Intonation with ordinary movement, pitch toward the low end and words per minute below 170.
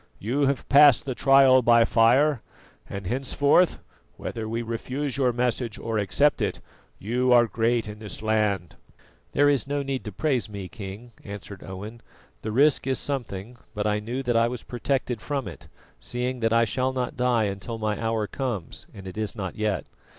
No: average, 3.5 semitones; low, 120 Hz; average, 180 wpm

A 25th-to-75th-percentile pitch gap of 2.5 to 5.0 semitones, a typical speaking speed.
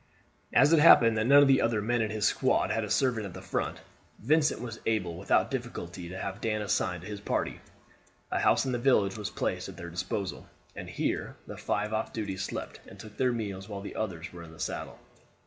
No: average, 3.6 semitones; fast, 225 wpm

